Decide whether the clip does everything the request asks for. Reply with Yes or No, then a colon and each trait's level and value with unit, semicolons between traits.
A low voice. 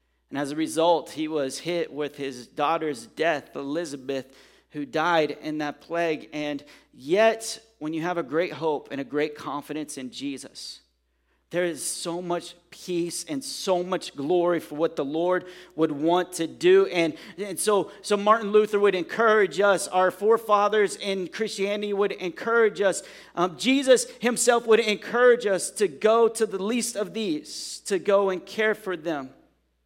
No: medium, 180 Hz